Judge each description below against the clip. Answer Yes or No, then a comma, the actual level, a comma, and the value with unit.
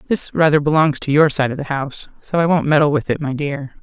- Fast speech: Yes, fast, 265 wpm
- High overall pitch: No, medium, 150 Hz